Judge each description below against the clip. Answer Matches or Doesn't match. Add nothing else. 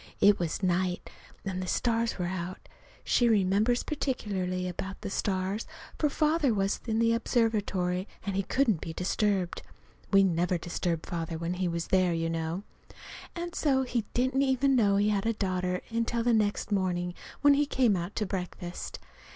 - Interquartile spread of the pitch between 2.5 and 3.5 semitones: Doesn't match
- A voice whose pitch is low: Doesn't match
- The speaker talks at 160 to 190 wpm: Matches